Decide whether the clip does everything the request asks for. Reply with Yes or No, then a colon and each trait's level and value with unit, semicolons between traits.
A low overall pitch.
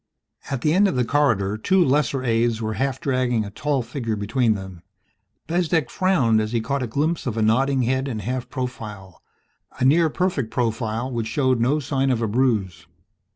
Yes: low, 125 Hz